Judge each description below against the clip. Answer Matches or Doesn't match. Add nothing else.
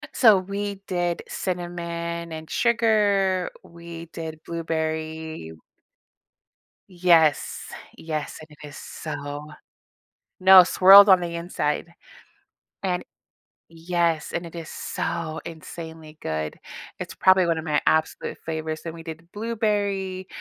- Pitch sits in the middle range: Matches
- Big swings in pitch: Doesn't match